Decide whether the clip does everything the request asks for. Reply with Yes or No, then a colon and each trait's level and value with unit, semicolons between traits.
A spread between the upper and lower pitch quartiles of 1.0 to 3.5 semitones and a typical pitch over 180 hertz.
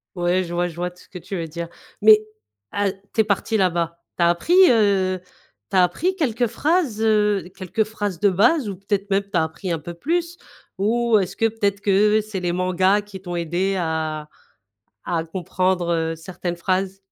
Yes: average, 3.2 semitones; high, 190 Hz